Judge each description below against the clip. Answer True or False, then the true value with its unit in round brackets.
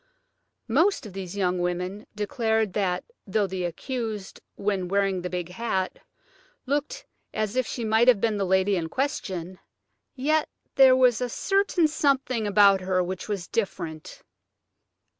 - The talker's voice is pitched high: True (205 Hz)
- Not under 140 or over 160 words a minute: True (145 wpm)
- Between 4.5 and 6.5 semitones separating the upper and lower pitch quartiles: True (5.0 semitones)